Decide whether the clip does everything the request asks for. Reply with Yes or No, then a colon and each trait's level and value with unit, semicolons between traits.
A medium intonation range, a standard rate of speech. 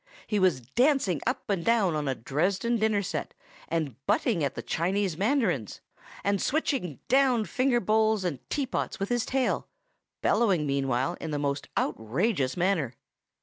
No: wide, 7.8 semitones; average, 150 wpm